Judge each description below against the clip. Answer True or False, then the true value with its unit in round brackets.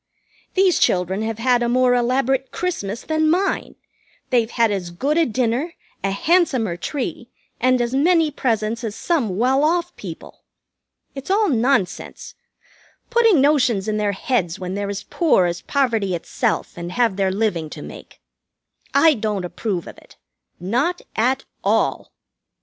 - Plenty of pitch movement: True (6.4 semitones)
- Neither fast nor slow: True (150 wpm)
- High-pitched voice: True (240 Hz)